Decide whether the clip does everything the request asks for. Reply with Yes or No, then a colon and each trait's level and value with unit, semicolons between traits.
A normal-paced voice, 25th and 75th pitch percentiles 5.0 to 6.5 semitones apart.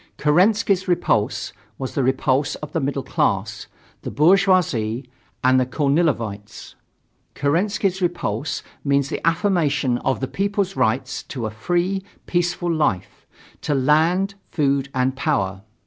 No: slow, 125 wpm; wide, 5.4 semitones